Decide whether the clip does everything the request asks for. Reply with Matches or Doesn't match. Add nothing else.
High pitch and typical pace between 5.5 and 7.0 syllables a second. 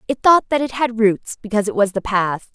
Matches